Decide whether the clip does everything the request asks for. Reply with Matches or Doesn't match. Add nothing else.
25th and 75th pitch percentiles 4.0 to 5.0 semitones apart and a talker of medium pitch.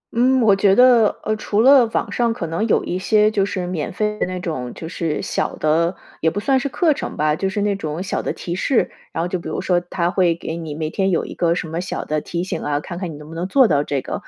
Matches